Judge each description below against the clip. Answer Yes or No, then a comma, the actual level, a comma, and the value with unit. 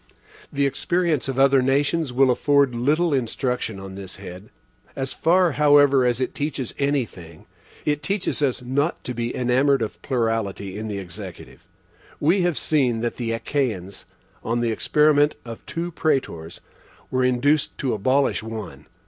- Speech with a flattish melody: No, average, 4.2 semitones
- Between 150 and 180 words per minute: Yes, average, 155 wpm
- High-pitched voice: No, low, 130 Hz